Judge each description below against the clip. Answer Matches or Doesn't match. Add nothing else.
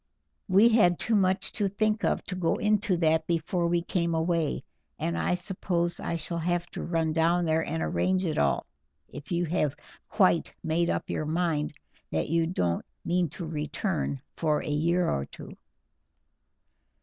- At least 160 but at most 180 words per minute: Matches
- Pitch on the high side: Doesn't match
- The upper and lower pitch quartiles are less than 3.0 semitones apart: Matches